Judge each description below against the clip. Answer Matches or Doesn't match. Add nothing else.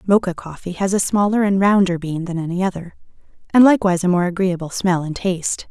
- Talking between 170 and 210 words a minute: Matches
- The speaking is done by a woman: Matches